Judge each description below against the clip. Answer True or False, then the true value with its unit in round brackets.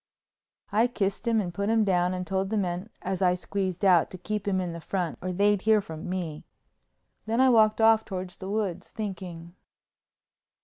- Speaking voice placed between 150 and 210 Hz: True (190 Hz)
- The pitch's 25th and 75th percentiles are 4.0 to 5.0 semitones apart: False (3.0 semitones)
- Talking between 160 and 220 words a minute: True (190 wpm)